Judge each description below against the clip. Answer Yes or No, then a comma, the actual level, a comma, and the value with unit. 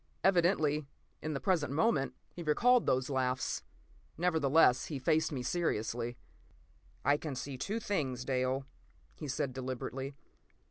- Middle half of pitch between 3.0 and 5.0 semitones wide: Yes, average, 3.9 semitones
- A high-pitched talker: No, medium, 140 Hz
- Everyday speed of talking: No, slow, 130 wpm